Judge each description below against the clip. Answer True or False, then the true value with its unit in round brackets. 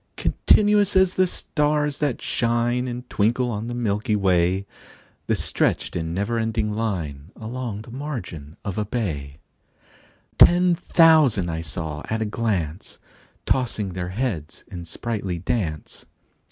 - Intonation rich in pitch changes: True (5.8 semitones)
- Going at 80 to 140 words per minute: True (135 wpm)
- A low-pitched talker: True (110 Hz)